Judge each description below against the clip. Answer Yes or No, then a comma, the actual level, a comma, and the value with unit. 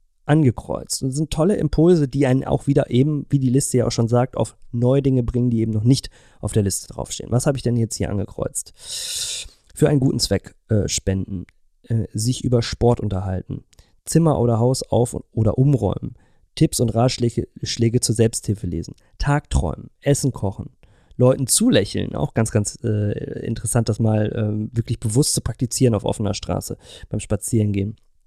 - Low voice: Yes, low, 120 Hz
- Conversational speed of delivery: Yes, average, 175 wpm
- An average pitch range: Yes, average, 4.0 semitones